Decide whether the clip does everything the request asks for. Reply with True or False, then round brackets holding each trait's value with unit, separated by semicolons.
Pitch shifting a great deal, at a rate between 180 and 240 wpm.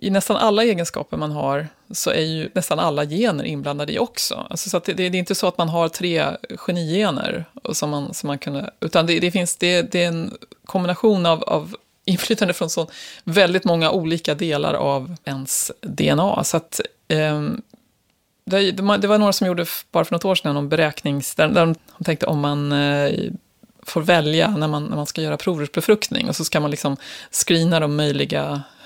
False (4.4 semitones; 185 wpm)